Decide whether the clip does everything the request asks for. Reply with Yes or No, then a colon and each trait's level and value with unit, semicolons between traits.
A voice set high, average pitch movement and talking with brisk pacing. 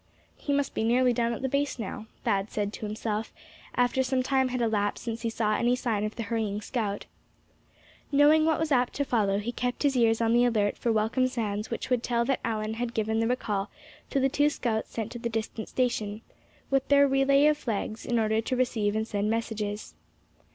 Yes: high, 230 Hz; average, 3.0 semitones; fast, 215 wpm